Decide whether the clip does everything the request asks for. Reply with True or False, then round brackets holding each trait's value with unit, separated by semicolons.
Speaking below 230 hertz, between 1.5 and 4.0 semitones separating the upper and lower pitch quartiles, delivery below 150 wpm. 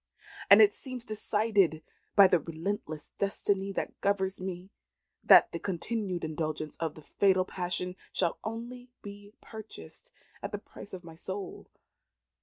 True (190 Hz; 3.4 semitones; 140 wpm)